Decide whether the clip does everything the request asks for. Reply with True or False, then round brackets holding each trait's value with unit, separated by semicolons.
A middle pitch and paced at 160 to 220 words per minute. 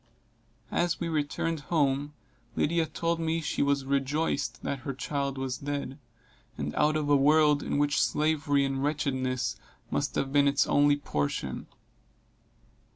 False (145 Hz; 145 wpm)